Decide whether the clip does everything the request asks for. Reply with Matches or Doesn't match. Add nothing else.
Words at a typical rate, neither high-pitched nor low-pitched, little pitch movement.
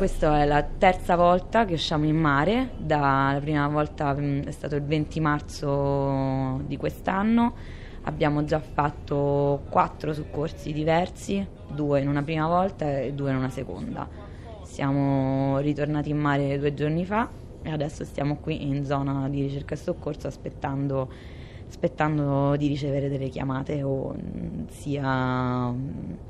Matches